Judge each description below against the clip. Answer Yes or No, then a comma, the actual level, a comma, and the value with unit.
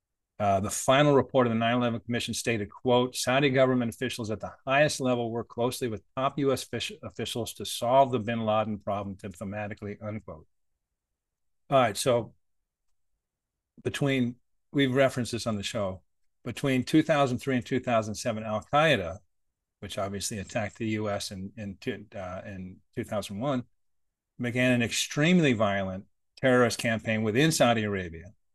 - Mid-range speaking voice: No, low, 110 Hz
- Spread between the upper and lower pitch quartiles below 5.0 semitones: Yes, average, 4.1 semitones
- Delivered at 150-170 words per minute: No, average, 140 wpm